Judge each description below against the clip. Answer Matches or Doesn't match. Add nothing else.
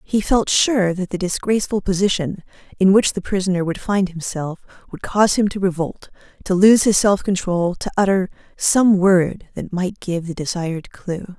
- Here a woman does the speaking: Matches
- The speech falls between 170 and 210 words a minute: Matches